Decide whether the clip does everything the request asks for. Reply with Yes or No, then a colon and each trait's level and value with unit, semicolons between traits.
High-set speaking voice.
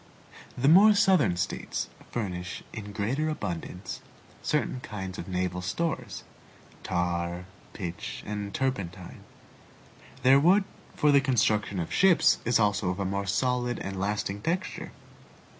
No: low, 105 Hz